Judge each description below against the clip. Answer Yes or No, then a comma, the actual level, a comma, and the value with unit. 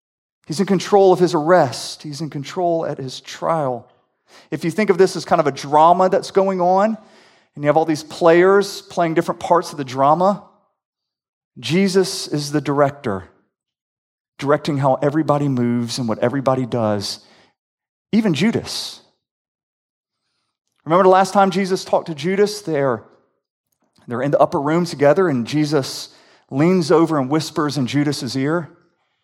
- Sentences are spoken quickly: No, average, 150 wpm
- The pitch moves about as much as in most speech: Yes, average, 4.7 semitones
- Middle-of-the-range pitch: Yes, medium, 160 Hz